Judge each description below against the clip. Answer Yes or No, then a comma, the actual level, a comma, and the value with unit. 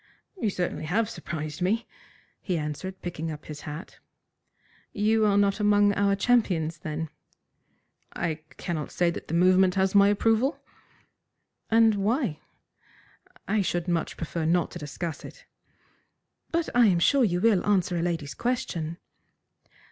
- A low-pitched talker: No, medium, 185 Hz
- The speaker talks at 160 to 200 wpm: No, average, 140 wpm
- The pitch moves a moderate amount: Yes, average, 4.2 semitones